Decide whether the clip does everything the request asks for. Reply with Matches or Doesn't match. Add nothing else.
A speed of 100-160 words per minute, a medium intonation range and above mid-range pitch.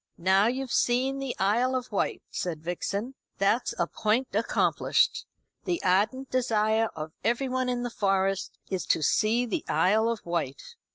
Matches